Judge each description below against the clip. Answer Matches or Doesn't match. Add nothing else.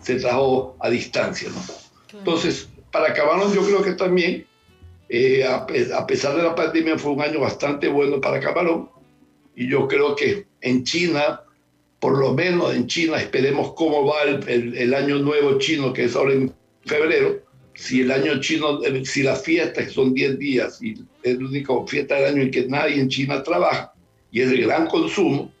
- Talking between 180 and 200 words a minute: Matches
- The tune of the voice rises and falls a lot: Matches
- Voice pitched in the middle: Matches